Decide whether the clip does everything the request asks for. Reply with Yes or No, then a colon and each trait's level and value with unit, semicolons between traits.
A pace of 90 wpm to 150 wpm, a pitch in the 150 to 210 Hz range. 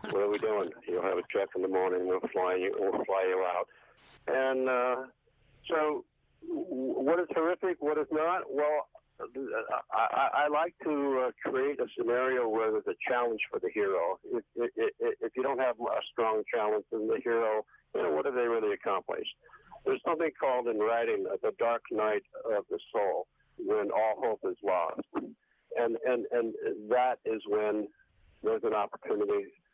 No: average, 175 wpm; high, 190 Hz